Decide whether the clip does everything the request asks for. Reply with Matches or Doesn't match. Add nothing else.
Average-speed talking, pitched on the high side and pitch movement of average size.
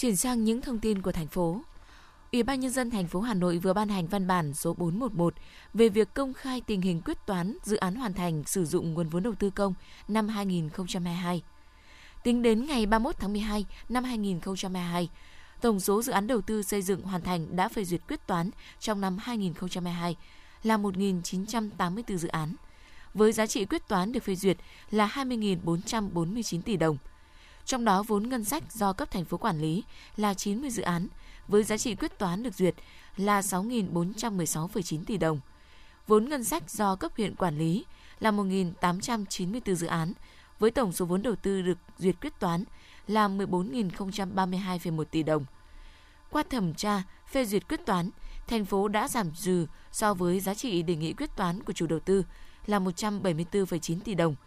Matches